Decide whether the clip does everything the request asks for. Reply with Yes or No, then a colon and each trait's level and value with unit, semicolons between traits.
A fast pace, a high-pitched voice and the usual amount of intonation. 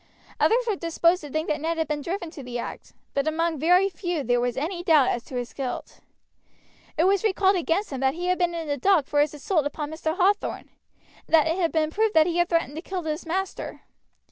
Yes: fast, 245 wpm; very high, 330 Hz; average, 3.3 semitones